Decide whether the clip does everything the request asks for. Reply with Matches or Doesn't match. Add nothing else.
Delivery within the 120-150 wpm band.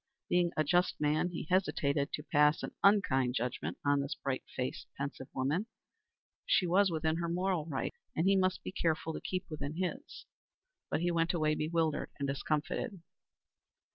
Doesn't match